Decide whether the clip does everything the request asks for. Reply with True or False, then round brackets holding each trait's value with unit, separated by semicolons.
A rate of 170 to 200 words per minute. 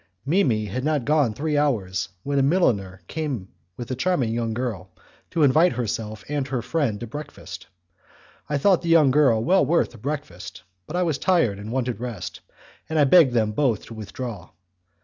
True (190 wpm)